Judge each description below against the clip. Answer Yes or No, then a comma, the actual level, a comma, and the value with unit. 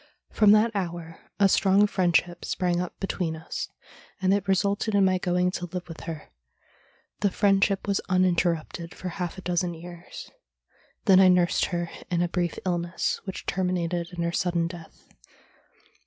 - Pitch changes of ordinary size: No, narrow, 1.9 semitones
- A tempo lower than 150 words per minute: No, average, 165 wpm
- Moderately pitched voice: Yes, medium, 180 Hz